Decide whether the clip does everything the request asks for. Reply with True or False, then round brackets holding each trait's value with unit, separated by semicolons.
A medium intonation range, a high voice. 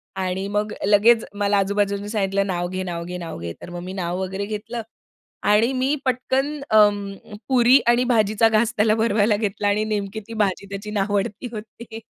False (2.3 semitones; 205 Hz)